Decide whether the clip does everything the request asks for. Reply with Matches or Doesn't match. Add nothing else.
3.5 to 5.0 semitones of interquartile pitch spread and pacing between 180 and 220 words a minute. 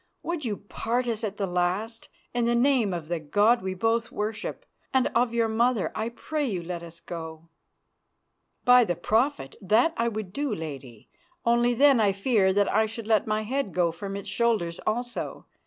Matches